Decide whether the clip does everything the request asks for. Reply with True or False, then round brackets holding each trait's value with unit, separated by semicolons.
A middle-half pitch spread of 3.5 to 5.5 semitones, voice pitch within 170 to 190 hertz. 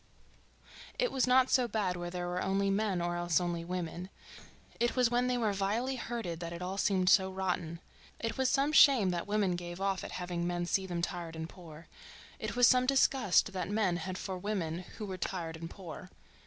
True (4.0 semitones; 185 Hz)